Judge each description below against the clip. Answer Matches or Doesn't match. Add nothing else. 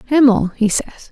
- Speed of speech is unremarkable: Matches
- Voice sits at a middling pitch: Doesn't match